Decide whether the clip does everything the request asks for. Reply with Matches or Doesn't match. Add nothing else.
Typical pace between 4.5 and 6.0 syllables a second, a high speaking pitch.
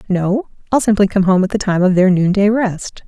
Matches